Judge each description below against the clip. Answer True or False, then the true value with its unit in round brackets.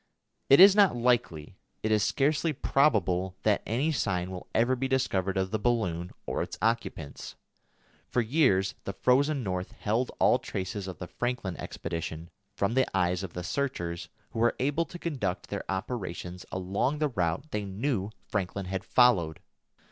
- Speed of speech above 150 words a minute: True (165 wpm)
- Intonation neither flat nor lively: False (5.9 semitones)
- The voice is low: True (105 Hz)